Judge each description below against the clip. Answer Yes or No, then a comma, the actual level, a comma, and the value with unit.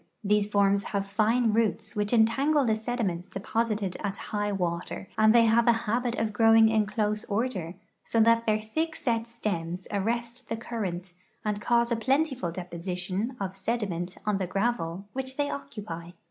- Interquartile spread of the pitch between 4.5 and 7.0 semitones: No, average, 3.2 semitones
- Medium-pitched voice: No, high, 215 Hz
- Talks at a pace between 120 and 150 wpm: No, average, 165 wpm